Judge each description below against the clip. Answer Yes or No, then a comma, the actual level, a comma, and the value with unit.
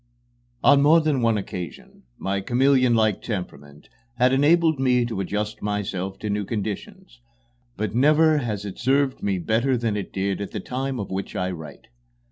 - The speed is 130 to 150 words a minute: No, average, 170 wpm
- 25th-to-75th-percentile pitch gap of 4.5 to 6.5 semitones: Yes, wide, 5.4 semitones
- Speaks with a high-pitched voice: No, low, 110 Hz